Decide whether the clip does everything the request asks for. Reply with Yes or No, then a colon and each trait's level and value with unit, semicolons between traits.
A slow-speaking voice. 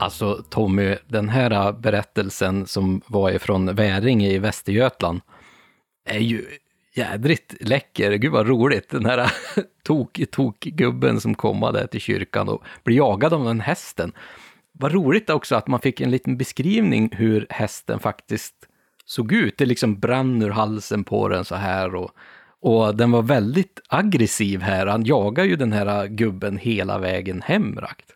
No: average, 155 wpm